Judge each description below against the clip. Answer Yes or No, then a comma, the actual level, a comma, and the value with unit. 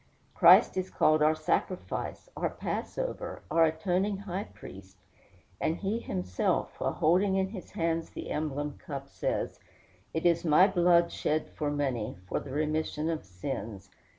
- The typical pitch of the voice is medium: Yes, medium, 160 Hz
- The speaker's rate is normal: Yes, average, 150 wpm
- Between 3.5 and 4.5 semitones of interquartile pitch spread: Yes, average, 3.9 semitones